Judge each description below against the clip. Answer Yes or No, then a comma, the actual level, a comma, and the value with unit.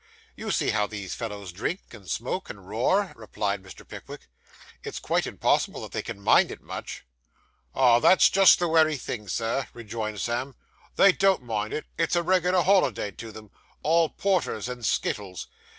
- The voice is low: Yes, low, 120 Hz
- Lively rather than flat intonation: Yes, wide, 8.3 semitones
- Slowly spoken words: No, average, 170 wpm